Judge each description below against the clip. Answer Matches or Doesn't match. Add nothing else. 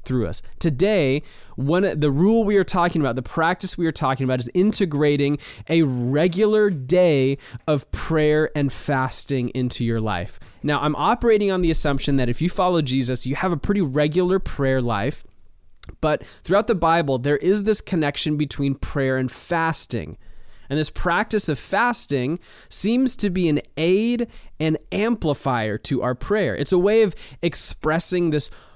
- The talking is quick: Doesn't match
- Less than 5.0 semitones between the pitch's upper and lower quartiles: Doesn't match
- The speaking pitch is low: Doesn't match